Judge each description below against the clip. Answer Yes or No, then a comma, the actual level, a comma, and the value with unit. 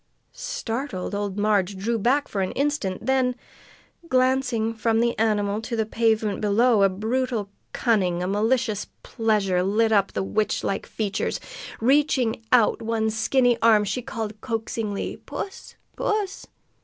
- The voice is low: No, high, 225 Hz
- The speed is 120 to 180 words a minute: Yes, average, 140 wpm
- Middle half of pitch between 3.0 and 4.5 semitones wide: Yes, average, 3.3 semitones